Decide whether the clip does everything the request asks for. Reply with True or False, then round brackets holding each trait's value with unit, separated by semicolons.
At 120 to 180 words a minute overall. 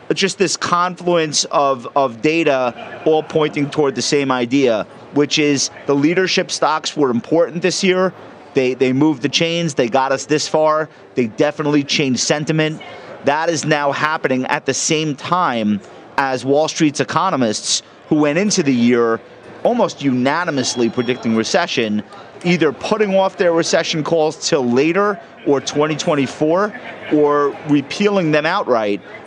True (145 wpm)